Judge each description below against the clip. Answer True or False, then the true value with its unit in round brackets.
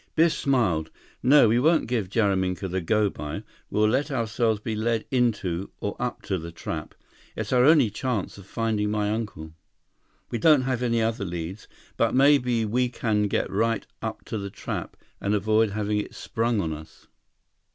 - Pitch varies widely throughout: False (3.5 semitones)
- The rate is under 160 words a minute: False (175 wpm)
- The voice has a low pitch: True (110 Hz)